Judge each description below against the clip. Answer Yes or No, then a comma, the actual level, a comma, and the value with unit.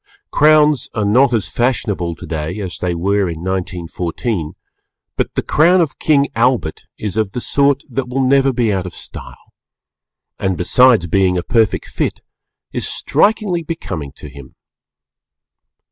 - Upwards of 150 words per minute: No, average, 145 wpm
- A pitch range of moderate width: No, wide, 7.1 semitones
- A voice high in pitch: No, low, 110 Hz